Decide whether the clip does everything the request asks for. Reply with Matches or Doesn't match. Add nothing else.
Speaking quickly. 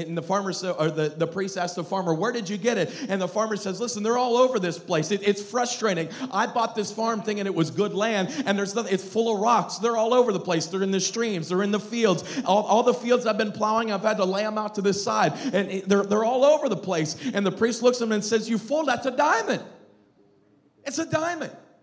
Matches